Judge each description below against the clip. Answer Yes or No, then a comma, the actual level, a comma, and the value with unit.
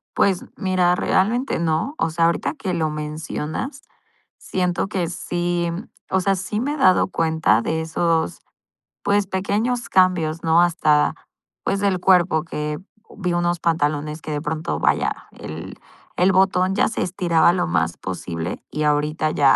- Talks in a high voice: No, medium, 170 Hz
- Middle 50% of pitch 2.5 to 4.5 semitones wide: Yes, average, 3.4 semitones